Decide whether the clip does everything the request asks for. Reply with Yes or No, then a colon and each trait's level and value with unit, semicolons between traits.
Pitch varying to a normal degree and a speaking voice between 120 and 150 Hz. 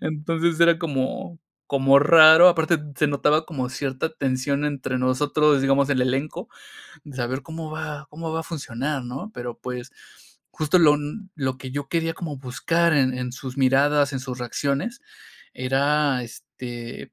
Yes: average, 3.3 semitones; medium, 140 Hz